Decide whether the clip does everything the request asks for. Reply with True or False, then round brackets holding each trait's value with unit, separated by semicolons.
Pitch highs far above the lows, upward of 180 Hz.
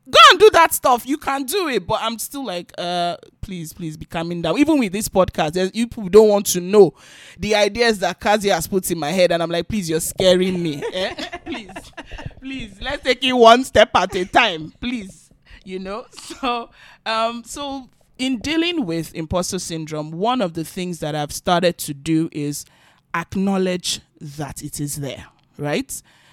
True (6.7 semitones; 190 Hz)